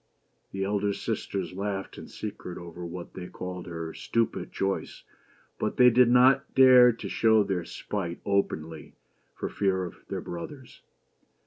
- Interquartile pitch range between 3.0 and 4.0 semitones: No, average, 4.6 semitones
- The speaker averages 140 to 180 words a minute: Yes, average, 145 wpm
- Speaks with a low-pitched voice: Yes, very low, 95 Hz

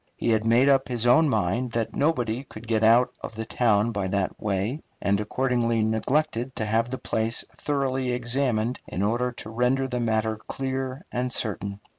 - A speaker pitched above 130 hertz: No, low, 120 Hz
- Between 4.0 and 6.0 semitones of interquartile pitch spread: No, average, 2.8 semitones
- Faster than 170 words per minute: Yes, average, 180 wpm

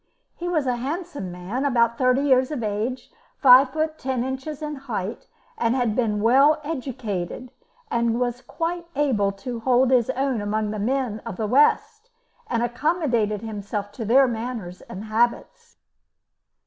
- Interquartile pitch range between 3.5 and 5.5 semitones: Yes, average, 3.9 semitones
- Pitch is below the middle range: No, high, 245 Hz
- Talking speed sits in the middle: Yes, average, 150 wpm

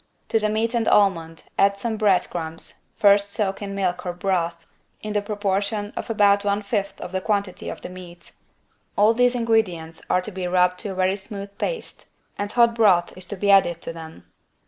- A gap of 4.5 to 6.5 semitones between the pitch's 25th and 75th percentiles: No, average, 2.7 semitones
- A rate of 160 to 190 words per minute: No, average, 200 wpm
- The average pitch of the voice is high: Yes, high, 200 Hz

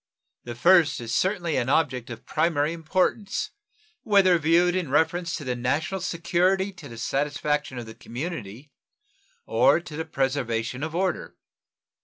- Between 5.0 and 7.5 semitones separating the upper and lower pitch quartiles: Yes, average, 5.3 semitones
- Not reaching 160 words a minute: Yes, average, 145 wpm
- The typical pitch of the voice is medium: Yes, medium, 155 Hz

